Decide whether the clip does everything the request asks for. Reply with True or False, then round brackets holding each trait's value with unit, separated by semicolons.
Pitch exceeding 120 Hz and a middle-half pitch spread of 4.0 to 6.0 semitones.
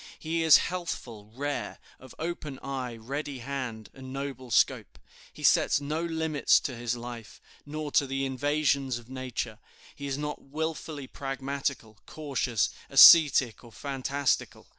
False (135 Hz; 2.9 semitones)